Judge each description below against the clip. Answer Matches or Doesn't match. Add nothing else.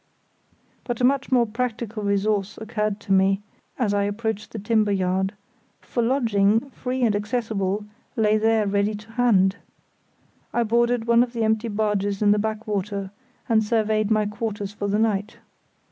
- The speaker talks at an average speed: Matches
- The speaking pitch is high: Matches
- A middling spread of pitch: Doesn't match